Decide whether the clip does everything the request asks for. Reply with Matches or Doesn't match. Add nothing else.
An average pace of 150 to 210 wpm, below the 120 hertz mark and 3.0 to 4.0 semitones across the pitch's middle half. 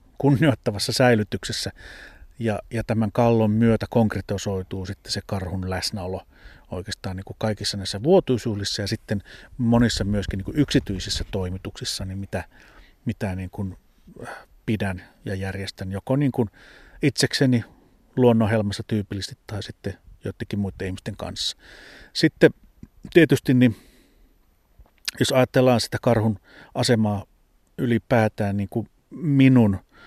Doesn't match